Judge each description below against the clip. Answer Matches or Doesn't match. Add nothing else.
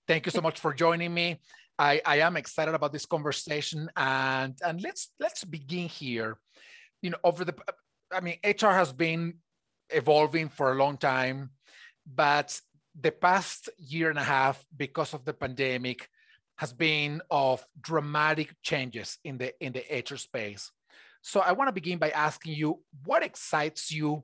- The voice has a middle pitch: Matches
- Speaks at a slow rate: Doesn't match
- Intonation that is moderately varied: Matches